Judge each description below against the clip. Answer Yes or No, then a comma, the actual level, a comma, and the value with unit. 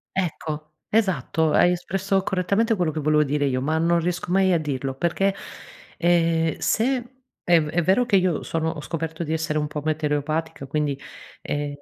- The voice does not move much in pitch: No, average, 3.2 semitones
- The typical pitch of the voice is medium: Yes, medium, 165 Hz